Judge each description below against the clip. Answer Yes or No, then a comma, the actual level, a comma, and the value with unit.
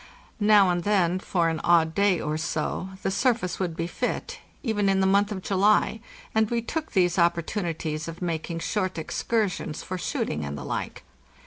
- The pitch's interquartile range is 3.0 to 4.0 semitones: Yes, average, 3.7 semitones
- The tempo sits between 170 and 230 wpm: Yes, average, 185 wpm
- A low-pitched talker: No, medium, 185 Hz